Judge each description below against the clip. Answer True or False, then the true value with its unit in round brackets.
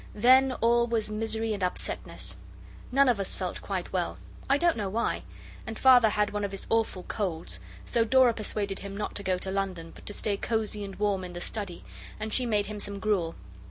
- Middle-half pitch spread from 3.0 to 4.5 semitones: False (2.6 semitones)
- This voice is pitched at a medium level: False (210 Hz)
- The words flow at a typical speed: False (210 wpm)